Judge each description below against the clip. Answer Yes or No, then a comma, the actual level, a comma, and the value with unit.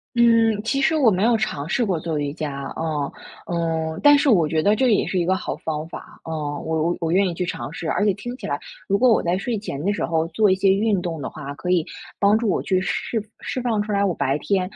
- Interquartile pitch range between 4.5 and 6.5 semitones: Yes, average, 5.0 semitones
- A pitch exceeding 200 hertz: No, medium, 185 Hz